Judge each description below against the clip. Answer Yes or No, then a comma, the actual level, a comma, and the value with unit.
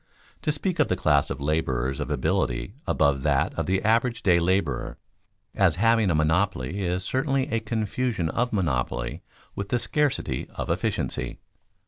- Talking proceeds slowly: No, average, 155 wpm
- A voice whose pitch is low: Yes, very low, 95 Hz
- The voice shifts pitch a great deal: Yes, wide, 7.5 semitones